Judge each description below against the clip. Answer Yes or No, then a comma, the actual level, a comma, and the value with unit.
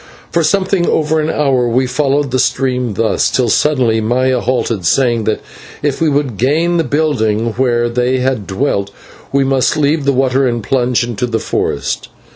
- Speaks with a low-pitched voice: Yes, low, 130 Hz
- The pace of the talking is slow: No, average, 175 wpm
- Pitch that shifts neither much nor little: Yes, average, 3.3 semitones